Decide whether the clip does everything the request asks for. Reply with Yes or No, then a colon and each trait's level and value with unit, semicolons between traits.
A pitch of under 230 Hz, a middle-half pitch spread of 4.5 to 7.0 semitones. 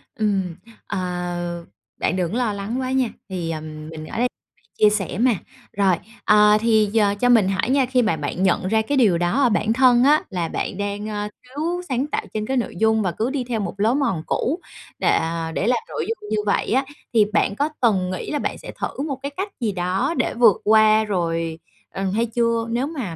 Yes: high, 215 Hz; average, 5.0 semitones